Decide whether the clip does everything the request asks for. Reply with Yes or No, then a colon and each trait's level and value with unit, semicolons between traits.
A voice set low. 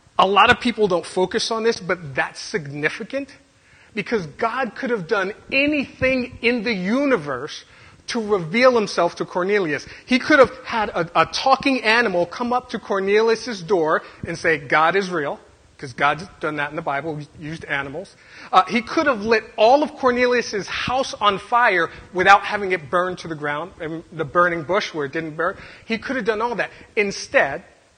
No: high, 210 Hz